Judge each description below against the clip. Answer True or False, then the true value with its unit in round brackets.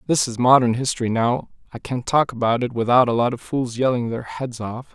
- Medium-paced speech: False (230 wpm)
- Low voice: True (120 Hz)